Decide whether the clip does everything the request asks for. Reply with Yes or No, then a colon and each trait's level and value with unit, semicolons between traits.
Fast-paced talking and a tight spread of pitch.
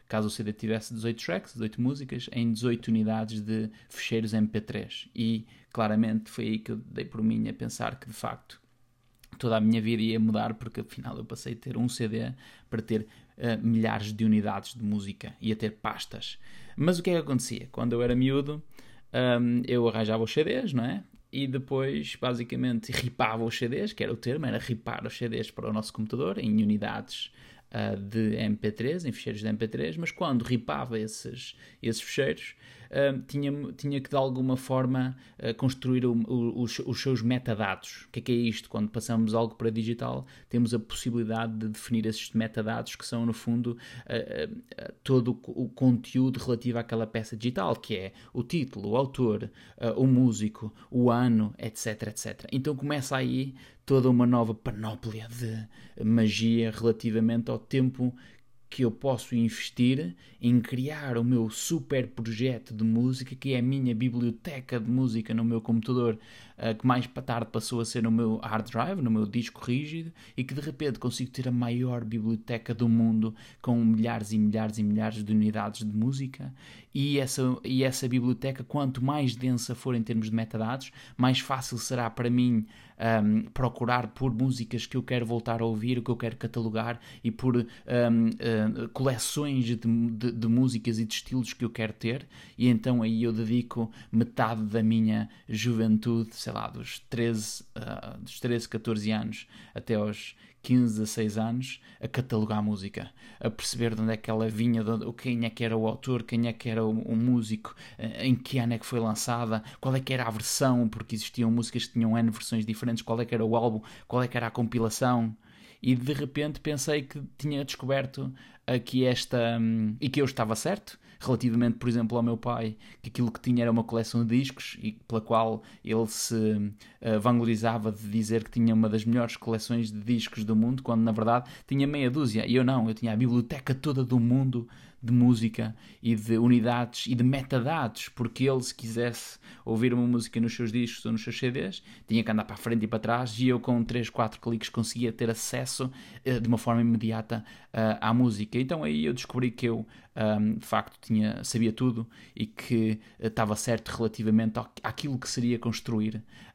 Yes: fast, 190 wpm; narrow, 2.0 semitones